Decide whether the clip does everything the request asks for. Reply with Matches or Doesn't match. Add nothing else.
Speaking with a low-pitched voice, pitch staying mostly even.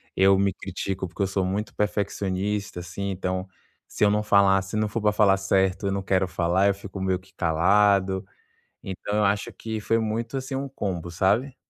Matches